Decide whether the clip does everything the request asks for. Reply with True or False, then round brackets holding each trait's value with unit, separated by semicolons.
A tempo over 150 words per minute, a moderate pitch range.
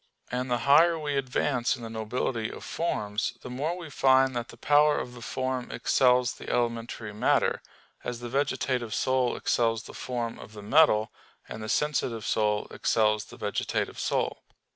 True (170 wpm; 3.0 semitones)